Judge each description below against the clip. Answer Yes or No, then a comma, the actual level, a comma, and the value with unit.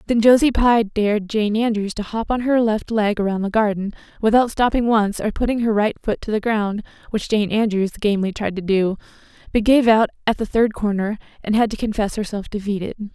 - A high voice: Yes, high, 215 Hz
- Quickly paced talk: Yes, fast, 210 wpm